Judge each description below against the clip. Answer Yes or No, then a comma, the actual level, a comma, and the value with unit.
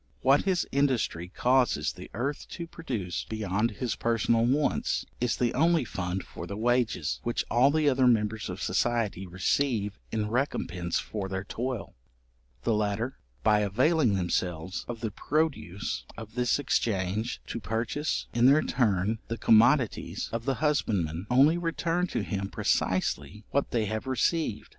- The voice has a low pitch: Yes, low, 115 Hz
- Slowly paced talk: No, average, 150 wpm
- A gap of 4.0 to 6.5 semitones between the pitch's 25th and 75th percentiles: Yes, average, 4.9 semitones